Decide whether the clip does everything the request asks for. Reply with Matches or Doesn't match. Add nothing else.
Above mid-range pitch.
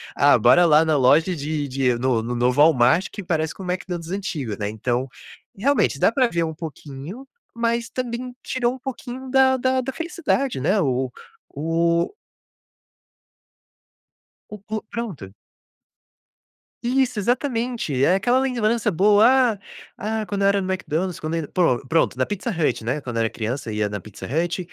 Doesn't match